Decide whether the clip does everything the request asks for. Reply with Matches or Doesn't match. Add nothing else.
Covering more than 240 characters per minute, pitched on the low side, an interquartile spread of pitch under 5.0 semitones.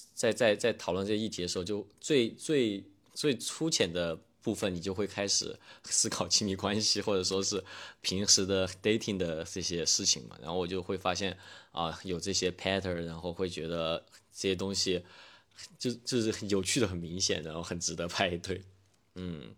Matches